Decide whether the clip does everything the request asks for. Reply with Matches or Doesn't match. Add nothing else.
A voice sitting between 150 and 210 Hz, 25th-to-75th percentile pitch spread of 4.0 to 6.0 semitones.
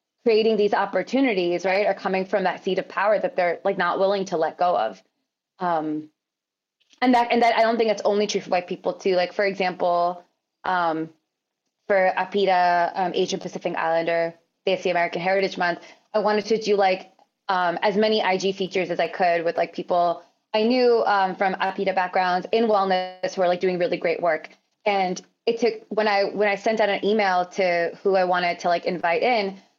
Doesn't match